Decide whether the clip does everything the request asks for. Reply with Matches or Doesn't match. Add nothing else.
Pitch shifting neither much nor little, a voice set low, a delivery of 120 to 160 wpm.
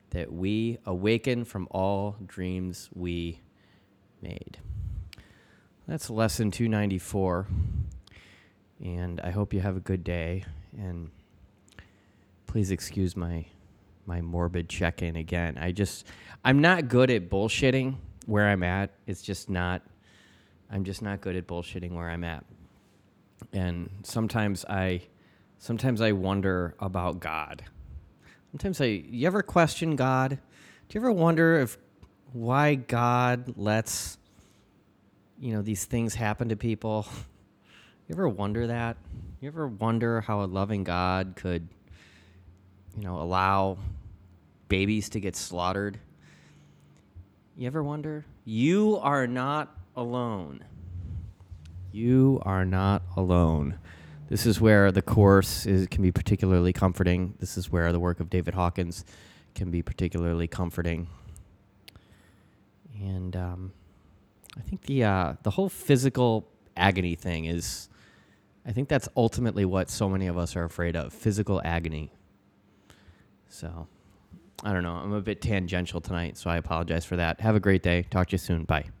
Matches